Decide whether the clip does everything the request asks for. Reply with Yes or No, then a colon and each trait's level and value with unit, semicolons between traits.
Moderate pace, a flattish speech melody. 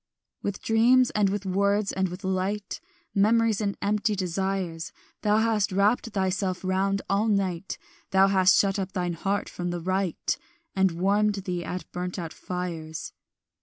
Yes: average, 155 wpm; narrow, 2.0 semitones